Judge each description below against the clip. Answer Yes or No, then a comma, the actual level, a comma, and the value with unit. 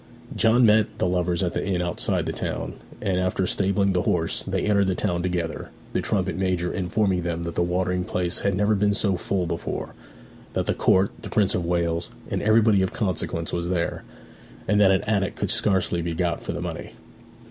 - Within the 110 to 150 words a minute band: No, average, 200 wpm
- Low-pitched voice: Yes, very low, 90 Hz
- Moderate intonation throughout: No, narrow, 2.3 semitones